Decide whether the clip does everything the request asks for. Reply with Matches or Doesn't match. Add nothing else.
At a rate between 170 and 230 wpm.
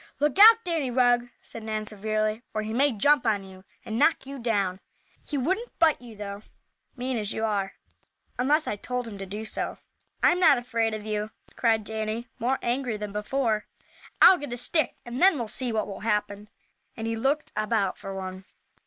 Matches